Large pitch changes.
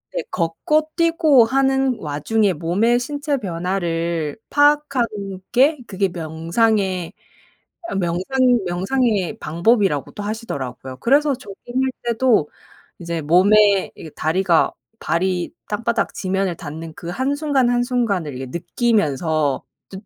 Yes: wide, 6.8 semitones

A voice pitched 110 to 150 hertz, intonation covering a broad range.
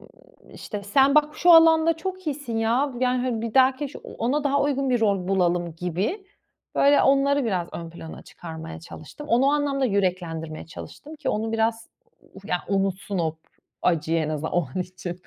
No: high, 225 Hz; wide, 8.0 semitones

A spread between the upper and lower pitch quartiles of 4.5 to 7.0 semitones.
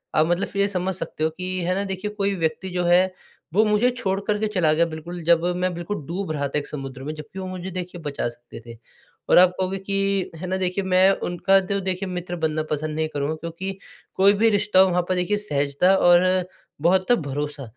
No: average, 3.3 semitones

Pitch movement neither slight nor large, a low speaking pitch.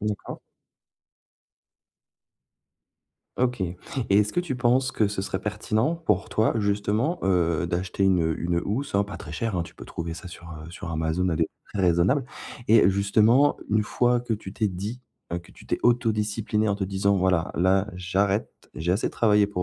Yes: average, 3.5 semitones; low, 100 Hz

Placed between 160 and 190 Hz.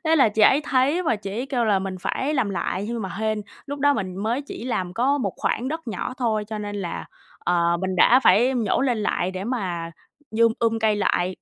No: high, 220 Hz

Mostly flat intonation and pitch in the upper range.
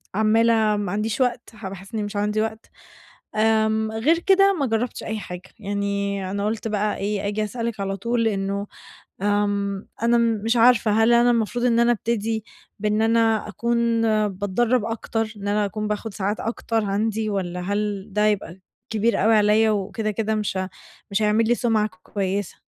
Yes: narrow, 1.9 semitones; high, 215 Hz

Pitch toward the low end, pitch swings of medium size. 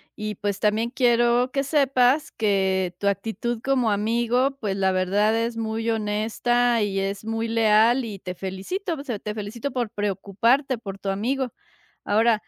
No: high, 225 Hz; average, 3.1 semitones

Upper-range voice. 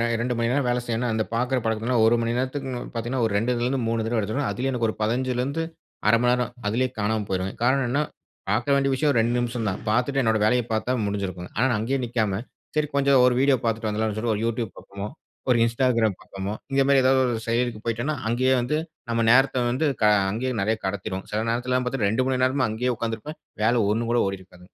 No: low, 120 Hz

